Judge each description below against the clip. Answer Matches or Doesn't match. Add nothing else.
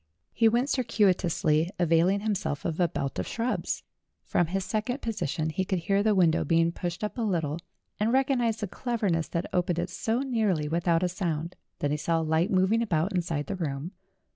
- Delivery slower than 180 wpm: Doesn't match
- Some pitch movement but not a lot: Matches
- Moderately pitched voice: Matches